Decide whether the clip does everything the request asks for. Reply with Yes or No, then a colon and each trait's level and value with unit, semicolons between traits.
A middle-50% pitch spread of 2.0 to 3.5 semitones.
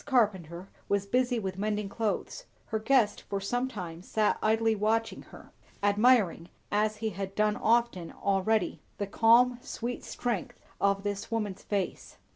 Yes: narrow, 2.5 semitones